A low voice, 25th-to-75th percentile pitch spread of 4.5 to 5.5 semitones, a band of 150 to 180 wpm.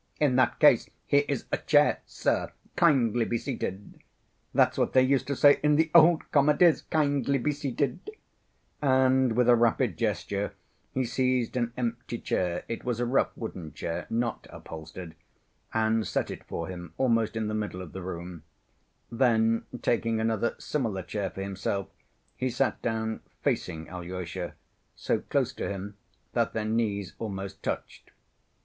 Yes: low, 115 Hz; average, 5.0 semitones; average, 160 wpm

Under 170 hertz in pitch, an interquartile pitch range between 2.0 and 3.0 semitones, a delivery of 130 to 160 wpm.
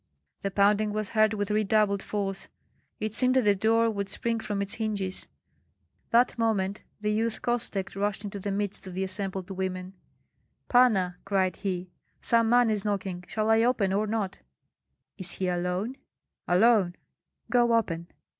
No: high, 205 Hz; narrow, 2.6 semitones; average, 155 wpm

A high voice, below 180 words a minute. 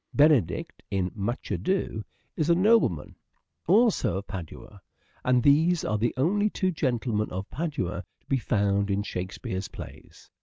No: low, 120 Hz; average, 155 wpm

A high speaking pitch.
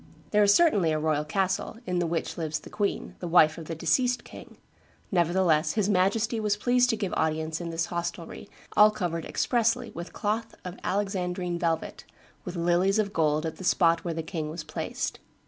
No: medium, 180 Hz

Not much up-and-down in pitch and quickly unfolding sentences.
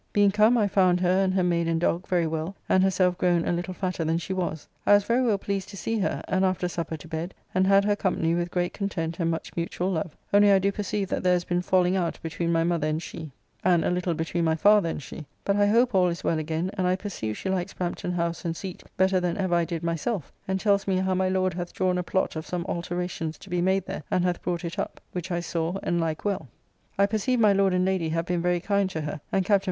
Yes: narrow, 2.3 semitones; fast, 265 wpm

